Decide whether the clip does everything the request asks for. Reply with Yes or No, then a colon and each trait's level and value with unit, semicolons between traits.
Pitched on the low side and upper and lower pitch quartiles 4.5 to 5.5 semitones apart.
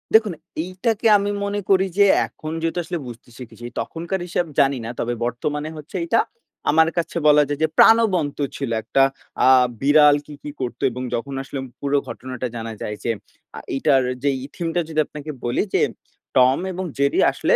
No: medium, 145 Hz; average, 4.9 semitones